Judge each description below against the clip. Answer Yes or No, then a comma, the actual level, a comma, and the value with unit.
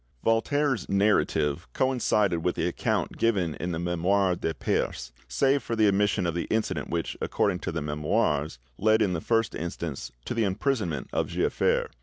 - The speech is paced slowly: No, average, 170 wpm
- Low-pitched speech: Yes, very low, 95 Hz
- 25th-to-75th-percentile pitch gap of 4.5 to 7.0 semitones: Yes, average, 5.1 semitones